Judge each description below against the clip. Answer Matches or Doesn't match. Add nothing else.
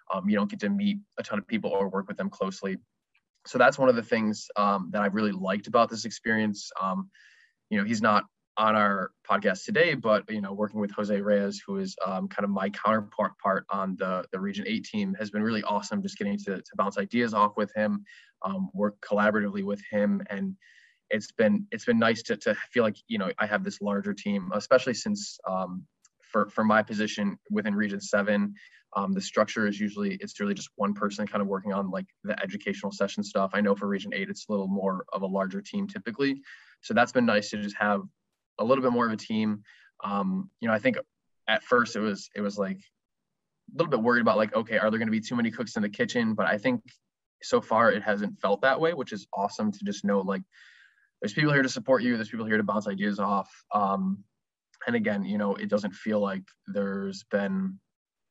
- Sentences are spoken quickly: Matches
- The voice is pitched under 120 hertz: Matches